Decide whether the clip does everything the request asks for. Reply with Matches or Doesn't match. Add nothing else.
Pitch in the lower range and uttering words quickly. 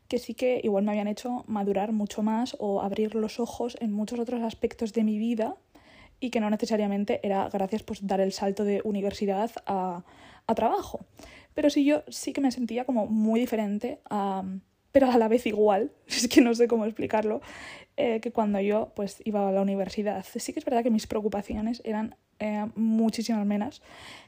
Doesn't match